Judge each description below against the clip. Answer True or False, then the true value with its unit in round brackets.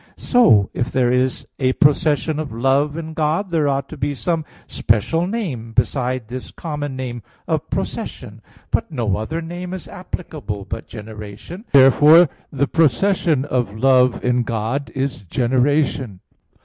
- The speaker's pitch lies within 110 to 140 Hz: True (135 Hz)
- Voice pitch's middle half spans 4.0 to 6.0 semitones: True (4.6 semitones)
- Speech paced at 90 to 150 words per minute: True (145 wpm)